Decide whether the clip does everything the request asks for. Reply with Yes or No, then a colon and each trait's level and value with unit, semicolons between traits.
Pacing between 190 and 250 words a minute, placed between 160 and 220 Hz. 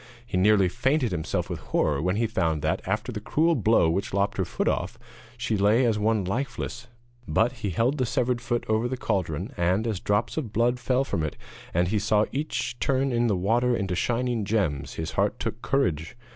No: fast, 205 wpm; low, 110 Hz